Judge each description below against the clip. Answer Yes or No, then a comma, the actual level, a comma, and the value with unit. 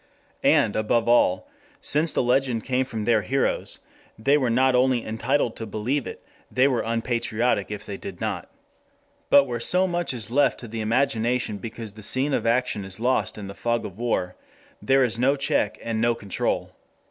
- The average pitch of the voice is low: Yes, low, 120 Hz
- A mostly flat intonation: No, average, 3.2 semitones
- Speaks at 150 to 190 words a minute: Yes, average, 185 wpm